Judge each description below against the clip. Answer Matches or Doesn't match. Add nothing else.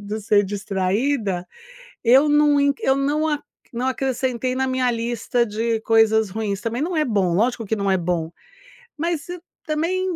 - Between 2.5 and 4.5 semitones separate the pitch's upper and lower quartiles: Doesn't match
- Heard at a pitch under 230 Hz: Doesn't match